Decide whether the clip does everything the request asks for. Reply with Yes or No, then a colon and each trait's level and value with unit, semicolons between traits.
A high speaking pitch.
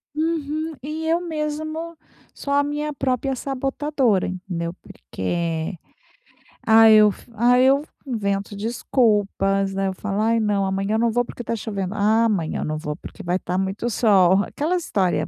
Yes: high, 220 Hz